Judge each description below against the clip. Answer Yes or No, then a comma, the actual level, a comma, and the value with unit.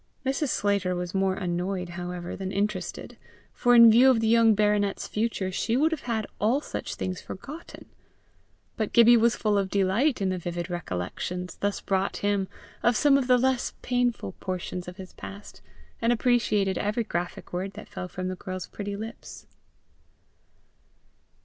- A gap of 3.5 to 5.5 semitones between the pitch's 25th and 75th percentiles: Yes, average, 4.1 semitones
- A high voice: Yes, high, 200 Hz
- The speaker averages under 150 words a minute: No, average, 165 wpm